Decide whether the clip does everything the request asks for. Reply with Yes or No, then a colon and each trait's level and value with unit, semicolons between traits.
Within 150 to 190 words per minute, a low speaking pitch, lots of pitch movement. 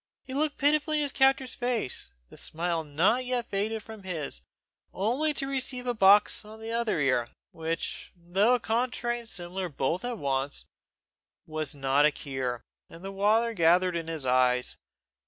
No: average, 170 wpm; high, 195 Hz; wide, 7.4 semitones